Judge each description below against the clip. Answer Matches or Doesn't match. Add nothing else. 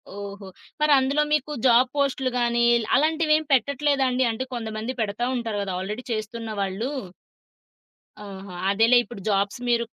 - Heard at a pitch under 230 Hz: Doesn't match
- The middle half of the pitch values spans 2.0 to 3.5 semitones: Doesn't match